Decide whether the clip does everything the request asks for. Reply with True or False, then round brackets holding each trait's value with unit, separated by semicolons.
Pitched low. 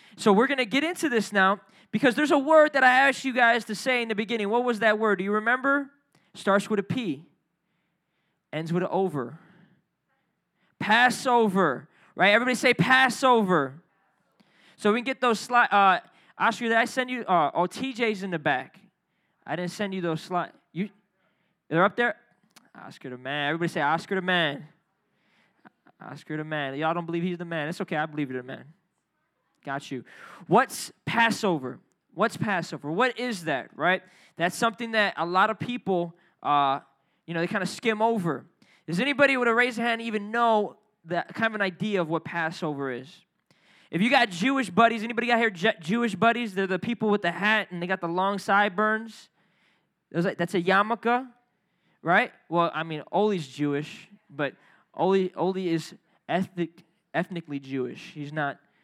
False (190 Hz)